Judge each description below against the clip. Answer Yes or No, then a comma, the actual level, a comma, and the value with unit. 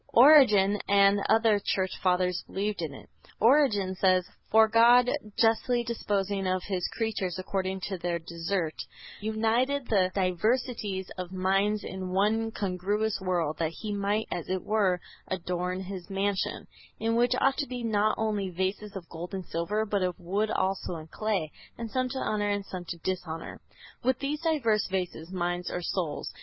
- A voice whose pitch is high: Yes, high, 195 Hz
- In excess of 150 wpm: Yes, average, 165 wpm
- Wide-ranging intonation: No, average, 3.3 semitones